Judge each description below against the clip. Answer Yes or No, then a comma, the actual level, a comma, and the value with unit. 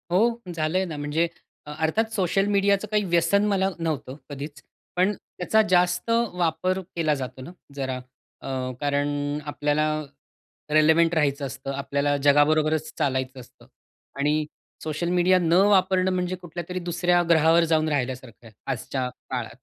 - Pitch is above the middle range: No, medium, 160 Hz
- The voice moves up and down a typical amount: Yes, average, 3.9 semitones